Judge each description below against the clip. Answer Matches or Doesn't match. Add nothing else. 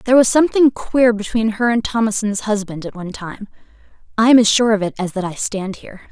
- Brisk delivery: Matches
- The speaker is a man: Doesn't match